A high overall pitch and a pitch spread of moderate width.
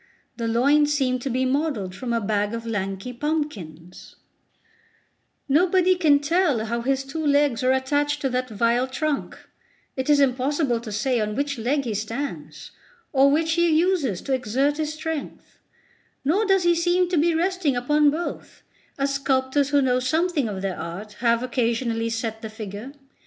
Yes: very high, 265 Hz; average, 4.5 semitones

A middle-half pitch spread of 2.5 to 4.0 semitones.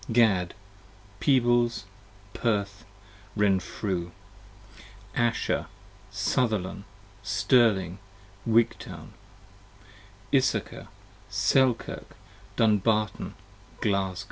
Yes: average, 3.3 semitones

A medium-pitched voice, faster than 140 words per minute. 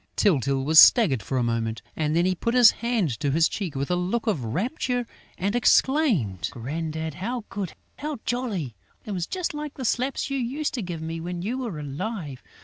Yes: medium, 180 Hz; average, 200 wpm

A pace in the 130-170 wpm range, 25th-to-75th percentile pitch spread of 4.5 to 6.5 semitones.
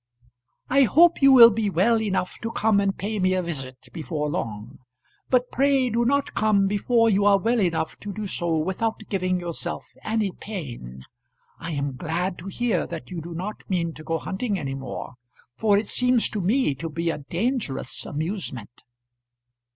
No: average, 180 wpm; wide, 5.5 semitones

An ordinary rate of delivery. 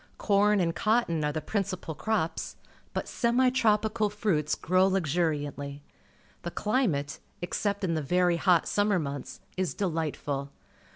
No: slow, 120 wpm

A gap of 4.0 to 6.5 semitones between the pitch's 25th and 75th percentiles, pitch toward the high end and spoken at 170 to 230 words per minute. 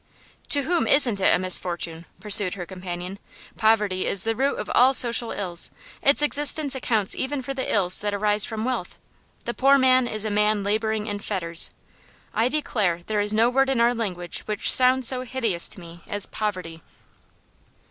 Yes: average, 5.2 semitones; high, 215 Hz; average, 180 wpm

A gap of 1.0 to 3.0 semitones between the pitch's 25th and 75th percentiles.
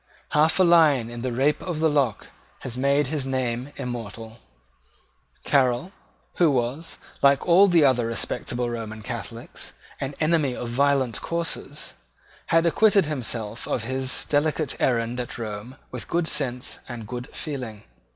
No: average, 4.2 semitones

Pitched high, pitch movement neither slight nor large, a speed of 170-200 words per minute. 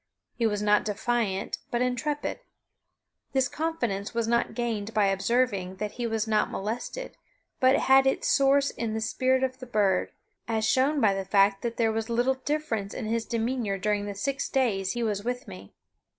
Yes: high, 230 Hz; average, 3.8 semitones; average, 180 wpm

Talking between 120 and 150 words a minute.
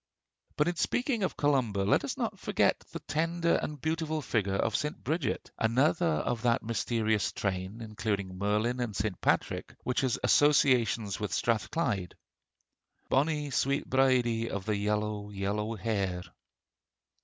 Yes: average, 145 wpm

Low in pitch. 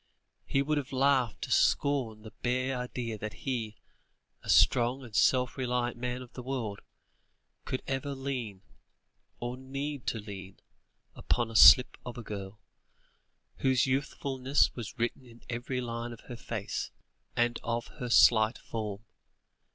Yes: low, 120 Hz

